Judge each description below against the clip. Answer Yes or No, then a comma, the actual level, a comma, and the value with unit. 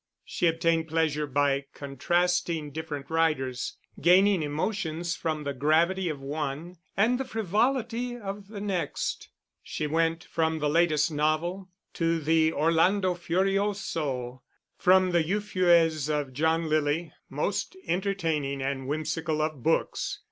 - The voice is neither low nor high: Yes, medium, 165 Hz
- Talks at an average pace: No, slow, 125 wpm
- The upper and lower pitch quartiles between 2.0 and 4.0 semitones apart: Yes, average, 3.4 semitones